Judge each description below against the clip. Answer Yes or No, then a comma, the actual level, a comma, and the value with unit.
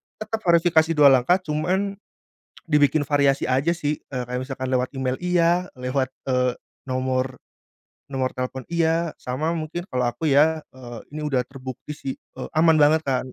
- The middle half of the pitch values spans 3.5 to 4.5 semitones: Yes, average, 3.9 semitones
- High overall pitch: No, medium, 145 Hz